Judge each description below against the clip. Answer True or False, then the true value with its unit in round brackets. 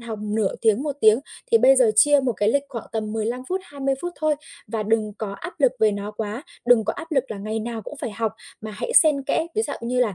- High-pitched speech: True (235 Hz)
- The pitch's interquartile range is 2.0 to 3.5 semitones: False (5.1 semitones)